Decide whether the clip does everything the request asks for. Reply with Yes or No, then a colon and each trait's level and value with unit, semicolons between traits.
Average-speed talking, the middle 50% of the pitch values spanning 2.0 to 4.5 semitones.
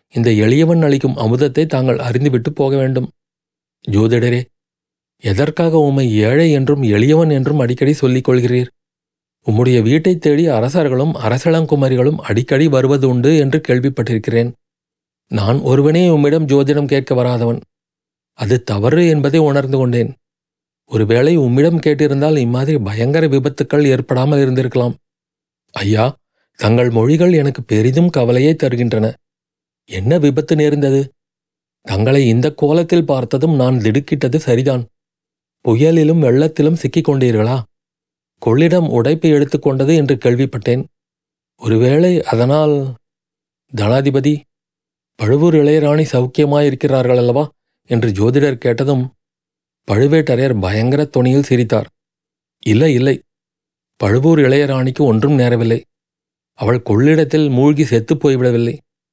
Yes: average, 100 wpm; average, 3.7 semitones